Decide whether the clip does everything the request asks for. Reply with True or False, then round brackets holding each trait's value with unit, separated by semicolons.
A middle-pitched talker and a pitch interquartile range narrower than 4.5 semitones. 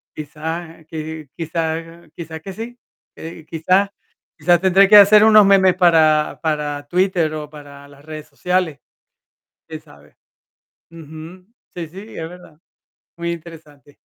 True (165 Hz; 2.8 semitones)